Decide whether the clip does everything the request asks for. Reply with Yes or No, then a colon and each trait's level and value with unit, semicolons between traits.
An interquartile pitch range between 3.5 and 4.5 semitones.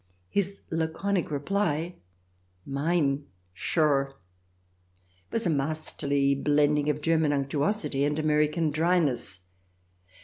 No: average, 2.8 semitones